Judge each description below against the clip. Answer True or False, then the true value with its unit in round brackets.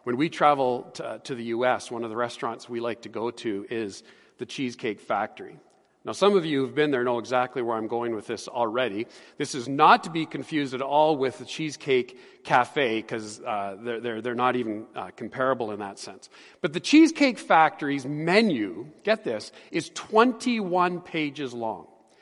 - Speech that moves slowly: False (185 wpm)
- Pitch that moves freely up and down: True (7.2 semitones)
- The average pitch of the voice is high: False (135 Hz)